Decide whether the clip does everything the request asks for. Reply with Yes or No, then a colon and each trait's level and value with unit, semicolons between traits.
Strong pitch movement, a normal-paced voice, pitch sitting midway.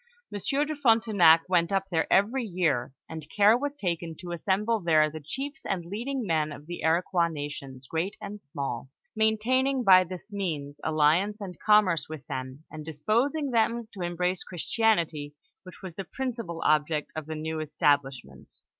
Yes: wide, 5.7 semitones; average, 175 wpm; medium, 175 Hz